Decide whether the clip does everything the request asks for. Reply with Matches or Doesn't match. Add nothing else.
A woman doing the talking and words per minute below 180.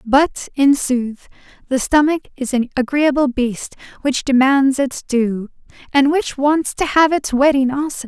Matches